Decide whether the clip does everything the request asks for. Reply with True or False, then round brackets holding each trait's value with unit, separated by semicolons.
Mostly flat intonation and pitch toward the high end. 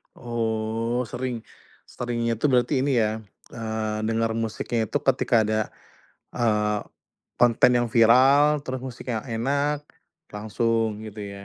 False (2.2 semitones; 115 Hz)